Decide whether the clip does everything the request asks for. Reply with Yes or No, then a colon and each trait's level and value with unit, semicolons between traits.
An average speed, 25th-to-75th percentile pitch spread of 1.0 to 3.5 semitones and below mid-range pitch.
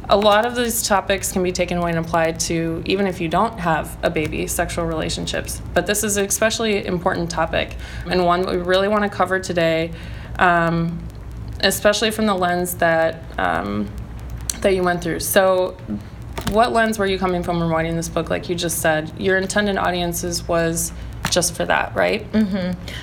No: average, 190 wpm; average, 3.1 semitones; medium, 175 Hz